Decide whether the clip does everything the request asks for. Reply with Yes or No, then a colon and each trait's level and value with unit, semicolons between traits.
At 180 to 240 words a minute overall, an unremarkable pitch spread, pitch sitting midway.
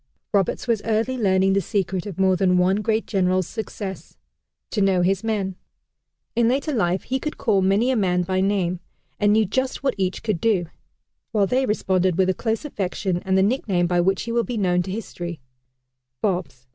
No: average, 195 wpm; average, 3.2 semitones; high, 195 Hz